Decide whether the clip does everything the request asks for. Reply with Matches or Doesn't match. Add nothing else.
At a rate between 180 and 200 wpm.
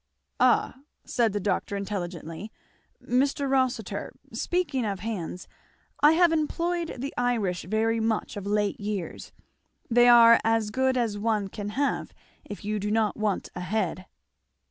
Doesn't match